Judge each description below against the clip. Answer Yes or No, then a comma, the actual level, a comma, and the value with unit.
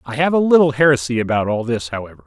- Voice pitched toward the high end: No, low, 130 Hz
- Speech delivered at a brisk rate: Yes, fast, 240 wpm